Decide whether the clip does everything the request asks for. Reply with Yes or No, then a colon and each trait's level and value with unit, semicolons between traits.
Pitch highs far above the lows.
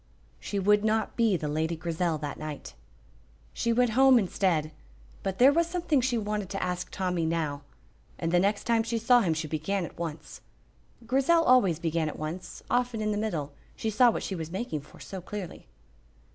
Yes: wide, 6.0 semitones